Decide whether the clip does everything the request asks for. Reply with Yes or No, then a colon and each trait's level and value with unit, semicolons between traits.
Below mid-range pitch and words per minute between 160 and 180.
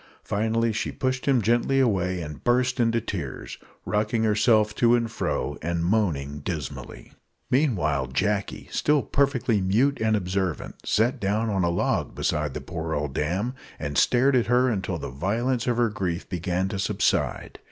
Yes: low, 105 Hz; average, 165 wpm